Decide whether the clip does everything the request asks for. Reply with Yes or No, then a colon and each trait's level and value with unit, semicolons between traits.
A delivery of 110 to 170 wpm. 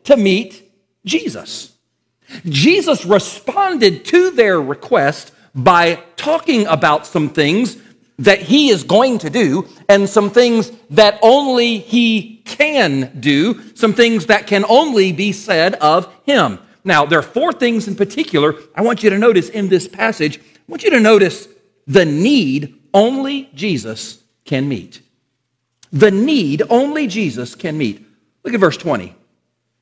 Yes: average, 145 wpm